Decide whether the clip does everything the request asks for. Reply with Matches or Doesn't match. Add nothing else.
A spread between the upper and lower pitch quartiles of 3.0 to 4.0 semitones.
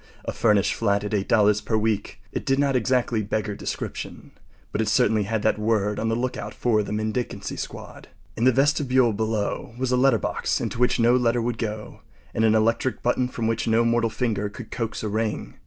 Doesn't match